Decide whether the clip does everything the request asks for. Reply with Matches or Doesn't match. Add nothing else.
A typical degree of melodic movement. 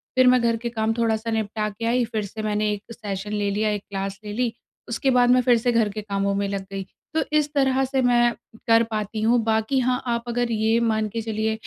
Doesn't match